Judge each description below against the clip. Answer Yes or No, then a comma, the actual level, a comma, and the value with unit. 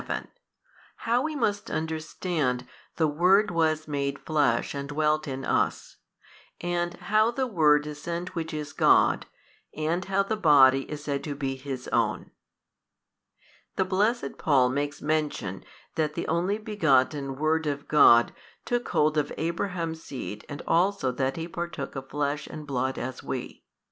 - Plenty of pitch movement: No, average, 3.7 semitones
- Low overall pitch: No, medium, 155 Hz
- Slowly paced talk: No, average, 150 wpm